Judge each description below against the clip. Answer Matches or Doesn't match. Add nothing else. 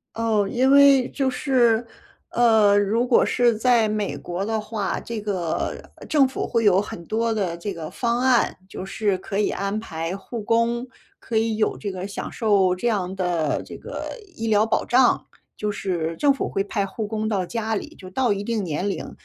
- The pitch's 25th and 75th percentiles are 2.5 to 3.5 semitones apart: Matches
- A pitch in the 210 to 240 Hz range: Matches